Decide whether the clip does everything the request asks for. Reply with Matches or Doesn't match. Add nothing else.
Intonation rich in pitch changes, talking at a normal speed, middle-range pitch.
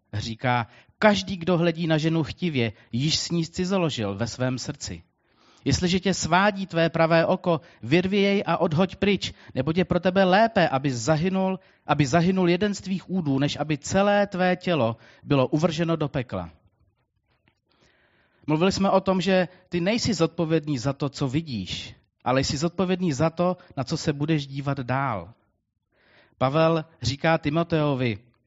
Matches